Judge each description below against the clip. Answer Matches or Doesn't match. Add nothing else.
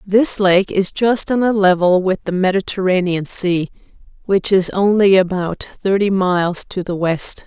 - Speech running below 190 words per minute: Matches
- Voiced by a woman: Matches